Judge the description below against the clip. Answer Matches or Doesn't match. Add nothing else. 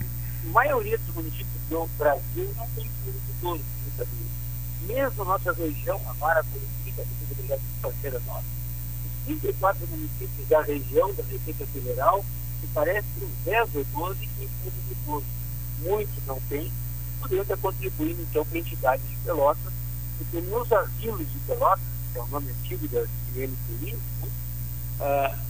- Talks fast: Doesn't match